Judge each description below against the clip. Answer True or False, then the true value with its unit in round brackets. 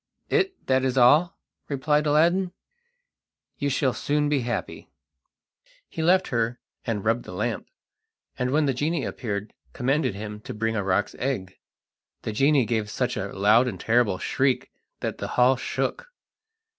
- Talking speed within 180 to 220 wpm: False (155 wpm)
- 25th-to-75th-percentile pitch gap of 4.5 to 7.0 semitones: True (4.8 semitones)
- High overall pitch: False (125 Hz)